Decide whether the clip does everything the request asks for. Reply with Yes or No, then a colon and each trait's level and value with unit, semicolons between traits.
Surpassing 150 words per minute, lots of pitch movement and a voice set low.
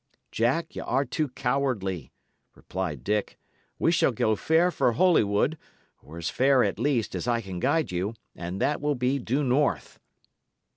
Yes: average, 160 wpm; wide, 6.2 semitones; low, 120 Hz